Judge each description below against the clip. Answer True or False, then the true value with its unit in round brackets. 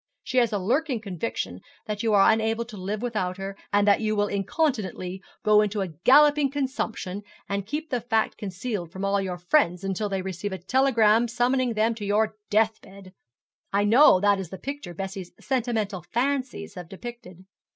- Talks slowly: False (180 wpm)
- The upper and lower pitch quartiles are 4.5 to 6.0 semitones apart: False (3.9 semitones)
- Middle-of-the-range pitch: False (210 Hz)